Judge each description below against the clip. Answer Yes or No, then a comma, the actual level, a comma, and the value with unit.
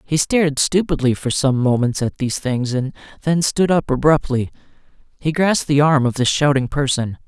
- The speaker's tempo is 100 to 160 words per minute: No, average, 180 wpm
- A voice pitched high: No, medium, 140 Hz